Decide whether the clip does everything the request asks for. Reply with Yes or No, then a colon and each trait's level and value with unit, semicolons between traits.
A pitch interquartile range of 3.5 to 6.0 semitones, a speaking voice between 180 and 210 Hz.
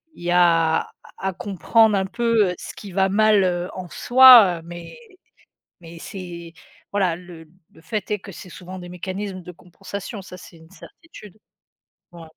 No: average, 2.8 semitones; medium, 185 Hz